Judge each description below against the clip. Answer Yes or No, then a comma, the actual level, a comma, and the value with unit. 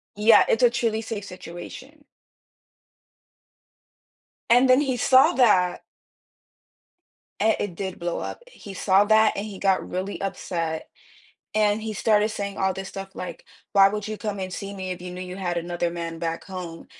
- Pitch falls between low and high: No, high, 195 Hz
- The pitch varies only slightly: No, average, 3.1 semitones